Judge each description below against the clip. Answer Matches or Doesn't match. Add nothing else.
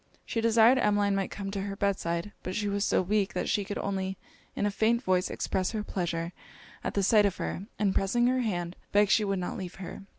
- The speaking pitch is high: Matches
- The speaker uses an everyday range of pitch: Doesn't match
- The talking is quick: Matches